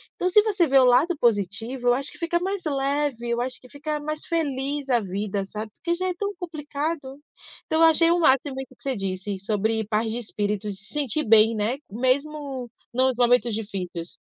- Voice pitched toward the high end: Yes, very high, 260 Hz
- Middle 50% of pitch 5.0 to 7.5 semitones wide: Yes, wide, 5.6 semitones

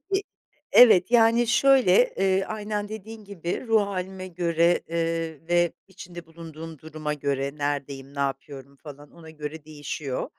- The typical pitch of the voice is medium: Yes, medium, 170 Hz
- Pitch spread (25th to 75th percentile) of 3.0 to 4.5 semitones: No, average, 5.2 semitones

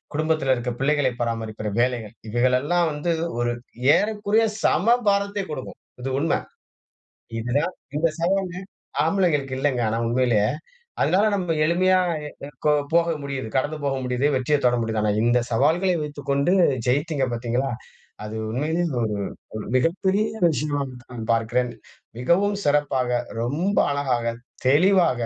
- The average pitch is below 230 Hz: Yes, medium, 140 Hz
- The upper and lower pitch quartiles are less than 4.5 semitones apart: No, wide, 5.5 semitones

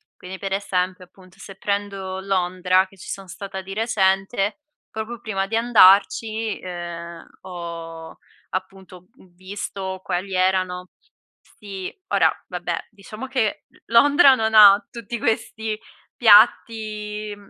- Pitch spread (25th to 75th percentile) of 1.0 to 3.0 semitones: Yes, average, 2.7 semitones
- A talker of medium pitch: No, high, 195 Hz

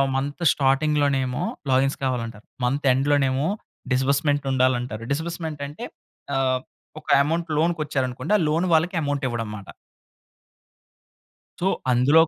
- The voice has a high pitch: No, medium, 140 Hz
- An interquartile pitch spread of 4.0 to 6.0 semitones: No, average, 3.0 semitones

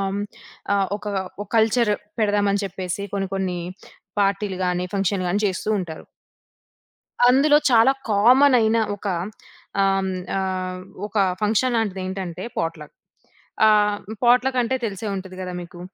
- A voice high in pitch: Yes, high, 200 Hz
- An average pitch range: Yes, average, 3.1 semitones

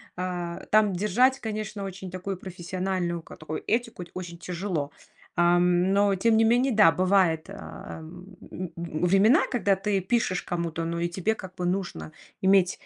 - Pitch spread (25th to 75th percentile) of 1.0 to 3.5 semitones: Yes, average, 2.8 semitones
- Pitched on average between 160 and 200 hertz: Yes, medium, 185 Hz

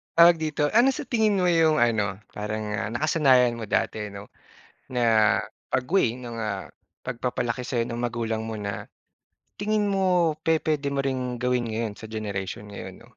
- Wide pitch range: Yes, wide, 6.1 semitones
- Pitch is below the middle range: Yes, low, 120 Hz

